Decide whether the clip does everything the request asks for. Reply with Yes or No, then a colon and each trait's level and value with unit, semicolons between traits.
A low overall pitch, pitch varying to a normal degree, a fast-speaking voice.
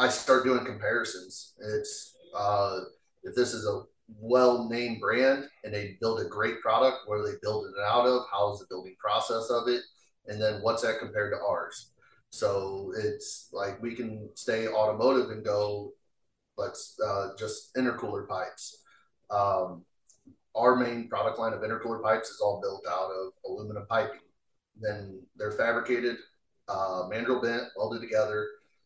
No: low, 115 Hz; average, 3.5 semitones; average, 160 wpm